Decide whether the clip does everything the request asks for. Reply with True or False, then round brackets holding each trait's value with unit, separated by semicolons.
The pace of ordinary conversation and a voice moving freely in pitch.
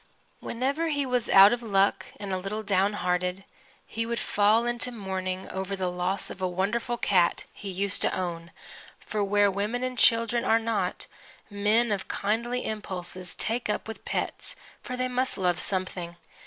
False (170 wpm; 3.8 semitones)